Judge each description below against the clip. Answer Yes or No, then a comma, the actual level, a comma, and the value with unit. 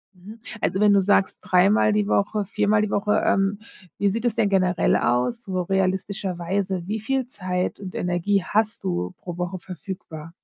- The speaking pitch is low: No, high, 195 Hz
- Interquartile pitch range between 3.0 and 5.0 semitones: No, narrow, 2.5 semitones